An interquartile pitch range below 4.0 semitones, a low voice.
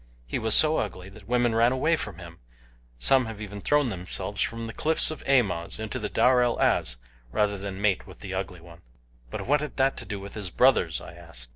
No: average, 4.7 semitones; low, 105 Hz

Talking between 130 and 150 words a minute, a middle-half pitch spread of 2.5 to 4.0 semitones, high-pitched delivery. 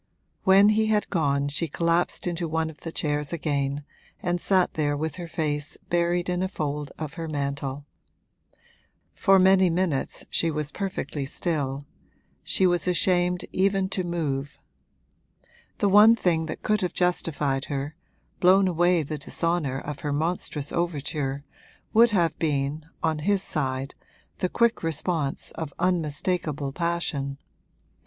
No: average, 140 wpm; average, 3.7 semitones; medium, 165 Hz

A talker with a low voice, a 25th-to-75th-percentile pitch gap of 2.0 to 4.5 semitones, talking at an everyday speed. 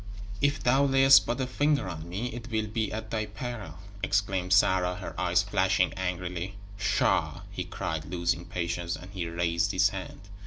No: very low, 95 Hz; average, 5.2 semitones; average, 170 wpm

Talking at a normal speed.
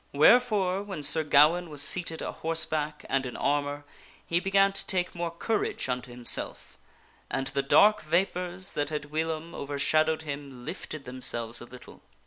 Yes: average, 155 wpm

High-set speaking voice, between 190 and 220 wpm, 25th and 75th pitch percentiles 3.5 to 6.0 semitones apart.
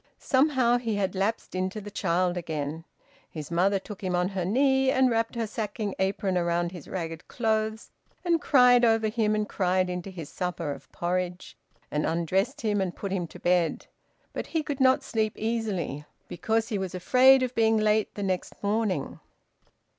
No: high, 200 Hz; average, 175 wpm; average, 4.1 semitones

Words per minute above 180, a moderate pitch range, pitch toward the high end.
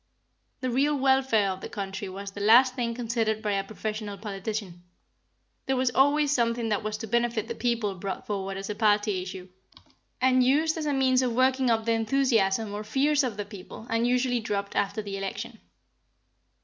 Yes: average, 190 wpm; average, 3.9 semitones; high, 225 Hz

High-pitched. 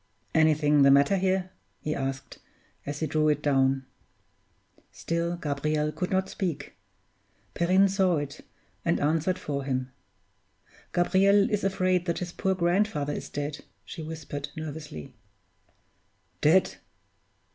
No: medium, 155 Hz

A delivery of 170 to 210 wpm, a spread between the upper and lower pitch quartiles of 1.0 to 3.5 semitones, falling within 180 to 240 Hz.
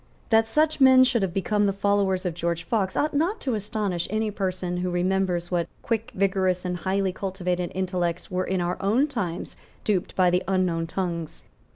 Yes: average, 185 wpm; average, 2.9 semitones; high, 190 Hz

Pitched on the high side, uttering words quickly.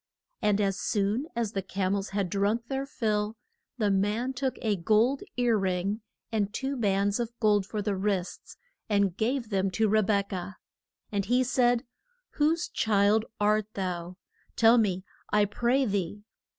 No: high, 210 Hz; average, 165 wpm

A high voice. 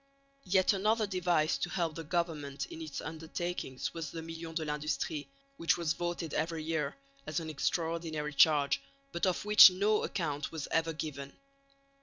No: medium, 165 Hz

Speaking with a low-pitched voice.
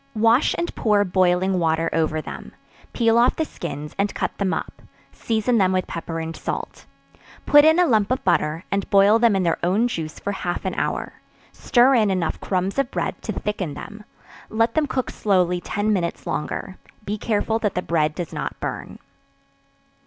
No: high, 200 Hz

